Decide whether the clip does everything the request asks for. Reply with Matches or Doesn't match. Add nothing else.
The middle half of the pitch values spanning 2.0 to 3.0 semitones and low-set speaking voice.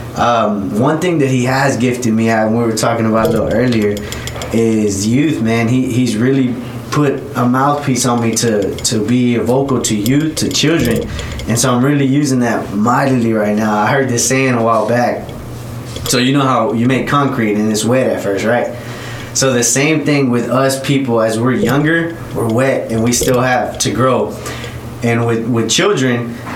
Matches